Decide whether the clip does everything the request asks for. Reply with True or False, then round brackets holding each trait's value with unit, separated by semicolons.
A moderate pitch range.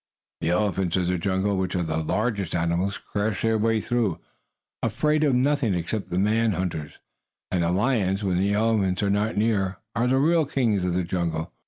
True (3.9 semitones)